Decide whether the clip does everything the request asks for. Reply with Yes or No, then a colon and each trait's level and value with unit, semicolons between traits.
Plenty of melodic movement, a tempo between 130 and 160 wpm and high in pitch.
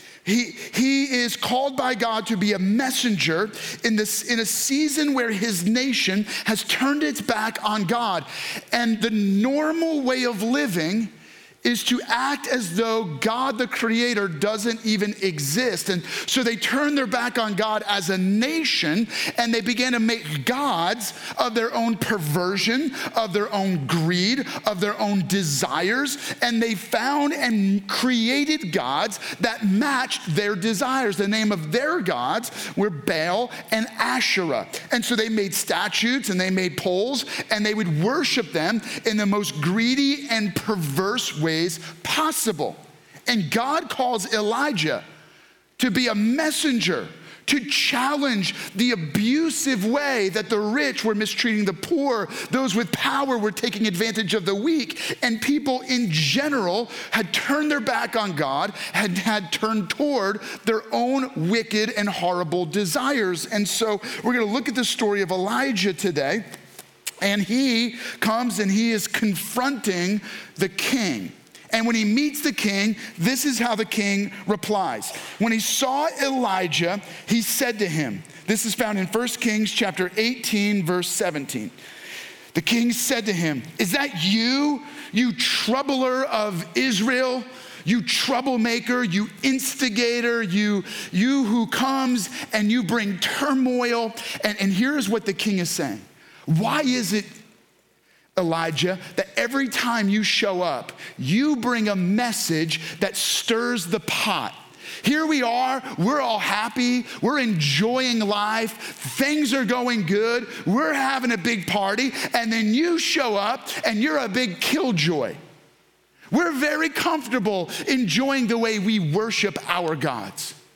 No: average, 3.9 semitones; average, 150 wpm; high, 225 Hz